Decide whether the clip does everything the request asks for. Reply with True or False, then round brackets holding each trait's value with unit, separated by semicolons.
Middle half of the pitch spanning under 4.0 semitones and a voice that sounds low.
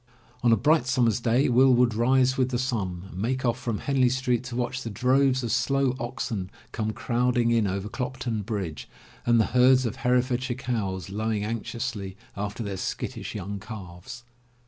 True (3.2 semitones; 120 Hz)